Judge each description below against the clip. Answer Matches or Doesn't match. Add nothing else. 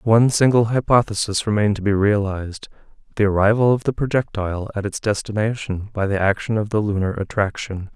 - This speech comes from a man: Matches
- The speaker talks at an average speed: Matches